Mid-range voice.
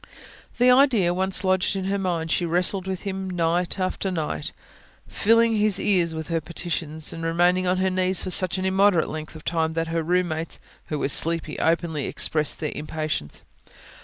Yes: medium, 175 Hz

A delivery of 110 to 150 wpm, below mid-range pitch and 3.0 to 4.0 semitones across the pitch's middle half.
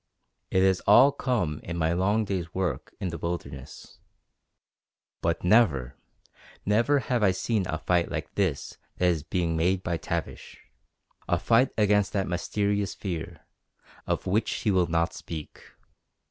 Yes: average, 145 wpm; very low, 90 Hz; average, 3.6 semitones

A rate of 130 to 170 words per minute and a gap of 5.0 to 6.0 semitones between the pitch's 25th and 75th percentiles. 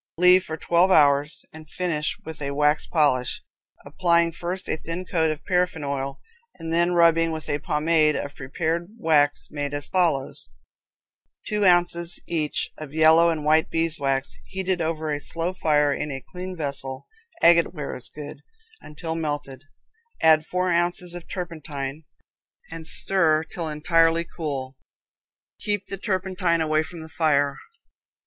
No: average, 145 wpm; narrow, 2.6 semitones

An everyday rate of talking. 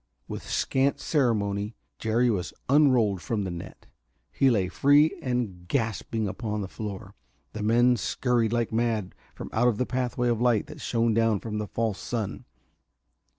Yes: average, 155 wpm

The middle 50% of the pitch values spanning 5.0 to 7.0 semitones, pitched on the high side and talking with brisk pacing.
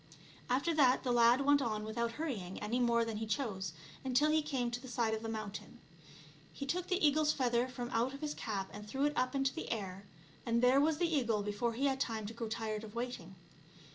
No: average, 3.9 semitones; high, 240 Hz; fast, 225 wpm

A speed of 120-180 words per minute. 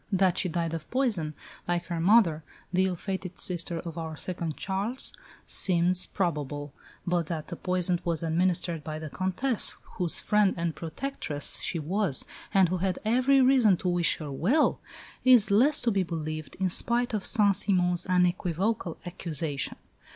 Yes: average, 160 wpm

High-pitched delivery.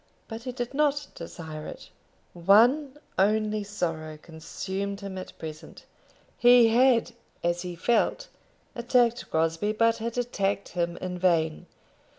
Yes: high, 200 Hz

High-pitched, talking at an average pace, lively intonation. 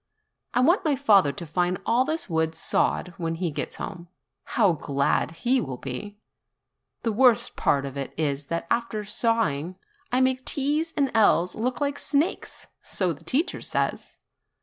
Yes: high, 205 Hz; average, 170 wpm; wide, 8.0 semitones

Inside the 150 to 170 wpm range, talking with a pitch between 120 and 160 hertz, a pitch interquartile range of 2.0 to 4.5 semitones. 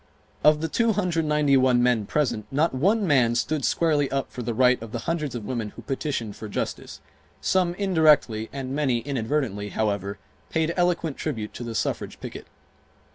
No: average, 165 wpm; low, 135 Hz; average, 5.3 semitones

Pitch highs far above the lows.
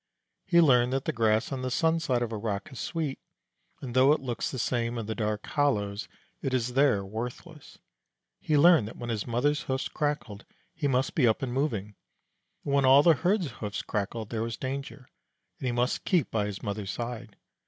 No: average, 4.2 semitones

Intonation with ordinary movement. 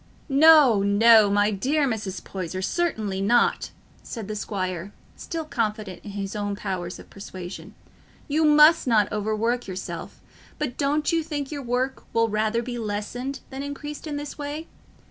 No: wide, 6.0 semitones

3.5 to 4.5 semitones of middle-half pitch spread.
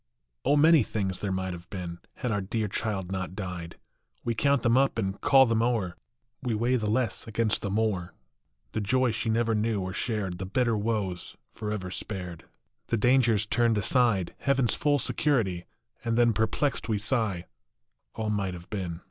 Yes: average, 3.8 semitones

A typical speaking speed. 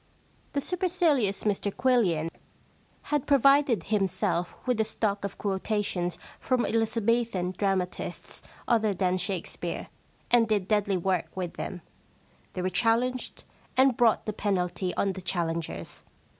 No: slow, 130 wpm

